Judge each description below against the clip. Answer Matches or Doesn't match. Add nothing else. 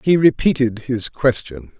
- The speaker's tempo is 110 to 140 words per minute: Matches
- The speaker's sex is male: Matches